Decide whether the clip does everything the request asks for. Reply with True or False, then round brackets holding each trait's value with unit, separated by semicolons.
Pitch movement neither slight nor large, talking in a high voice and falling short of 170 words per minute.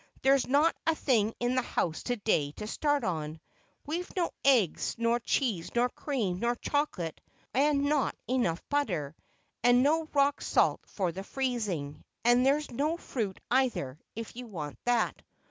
False (6.6 semitones; 245 Hz; 160 wpm)